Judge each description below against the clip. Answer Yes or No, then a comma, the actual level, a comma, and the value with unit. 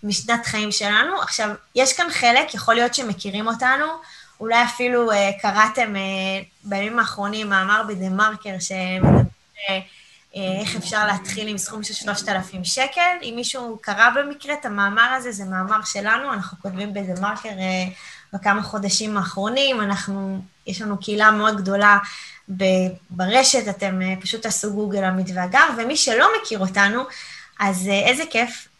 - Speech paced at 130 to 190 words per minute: Yes, average, 145 wpm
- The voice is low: No, high, 210 Hz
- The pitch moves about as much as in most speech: Yes, average, 3.1 semitones